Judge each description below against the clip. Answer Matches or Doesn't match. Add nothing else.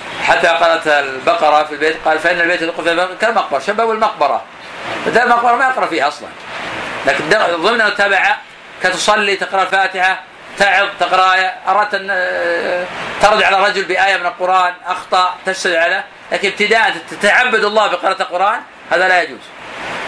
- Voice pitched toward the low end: Doesn't match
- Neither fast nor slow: Doesn't match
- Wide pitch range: Doesn't match